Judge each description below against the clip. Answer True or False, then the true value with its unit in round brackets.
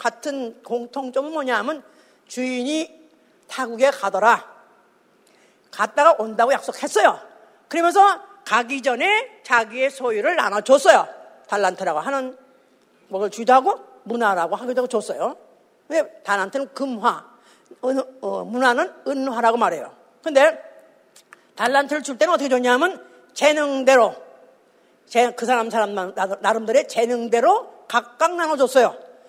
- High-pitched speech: True (255 Hz)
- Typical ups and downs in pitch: True (4.3 semitones)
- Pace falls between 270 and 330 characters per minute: True (275 characters per minute)